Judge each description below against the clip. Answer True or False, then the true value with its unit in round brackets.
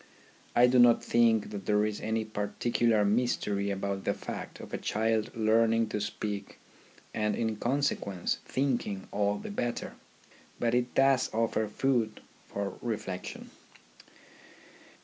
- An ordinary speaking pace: False (130 wpm)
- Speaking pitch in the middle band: False (110 Hz)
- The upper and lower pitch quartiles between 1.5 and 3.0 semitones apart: True (2.6 semitones)